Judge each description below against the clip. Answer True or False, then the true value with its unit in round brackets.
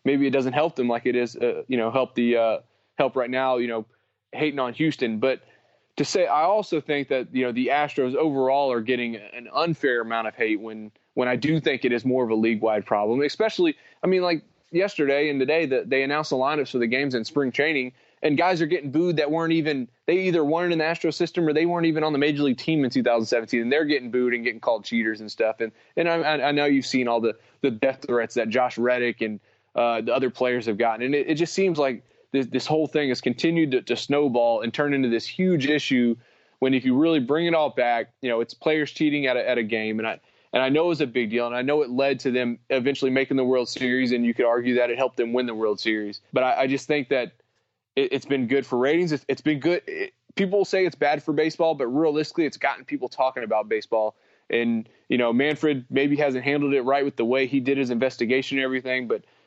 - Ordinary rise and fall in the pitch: True (4.0 semitones)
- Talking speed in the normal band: False (255 wpm)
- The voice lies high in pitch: False (135 Hz)